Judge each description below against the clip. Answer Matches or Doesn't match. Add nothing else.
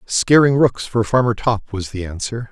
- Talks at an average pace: Matches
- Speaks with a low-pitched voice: Matches